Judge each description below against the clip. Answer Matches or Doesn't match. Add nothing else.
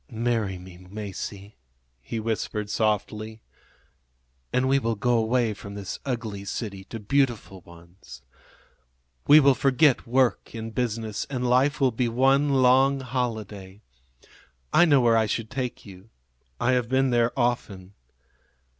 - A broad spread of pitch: Doesn't match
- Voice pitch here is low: Matches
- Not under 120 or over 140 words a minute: Matches